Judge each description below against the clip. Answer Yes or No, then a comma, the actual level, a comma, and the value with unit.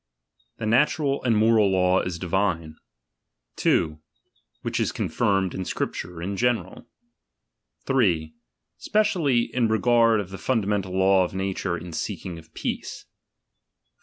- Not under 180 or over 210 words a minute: No, slow, 135 wpm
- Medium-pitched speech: No, very low, 95 Hz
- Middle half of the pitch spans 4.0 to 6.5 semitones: Yes, average, 4.4 semitones